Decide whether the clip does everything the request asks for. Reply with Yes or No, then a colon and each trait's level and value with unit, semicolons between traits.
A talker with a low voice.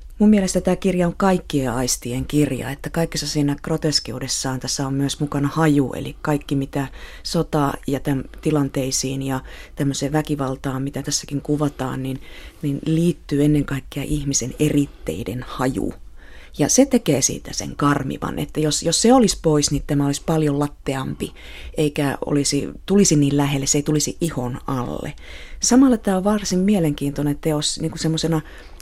No: medium, 145 Hz